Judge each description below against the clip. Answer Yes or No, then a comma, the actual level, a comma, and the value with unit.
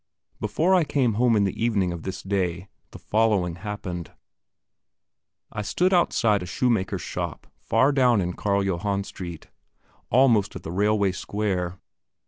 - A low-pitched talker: Yes, low, 100 Hz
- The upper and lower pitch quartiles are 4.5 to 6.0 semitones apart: No, average, 3.7 semitones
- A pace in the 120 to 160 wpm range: Yes, average, 145 wpm